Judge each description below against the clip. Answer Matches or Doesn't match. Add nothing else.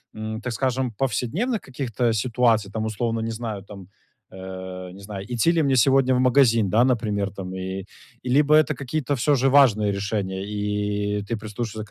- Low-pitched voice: Matches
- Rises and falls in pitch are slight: Doesn't match